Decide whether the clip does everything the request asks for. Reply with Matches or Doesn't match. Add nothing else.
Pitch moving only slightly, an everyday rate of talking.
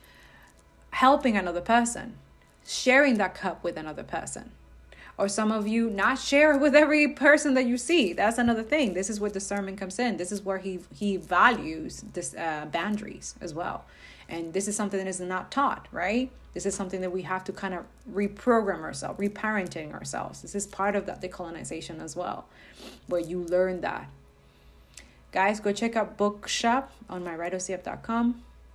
Doesn't match